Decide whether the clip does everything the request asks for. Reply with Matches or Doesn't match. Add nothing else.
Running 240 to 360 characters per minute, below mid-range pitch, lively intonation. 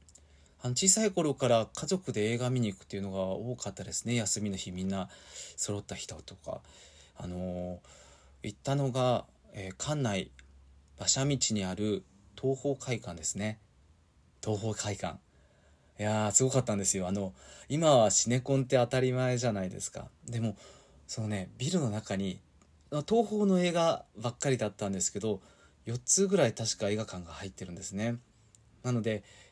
Doesn't match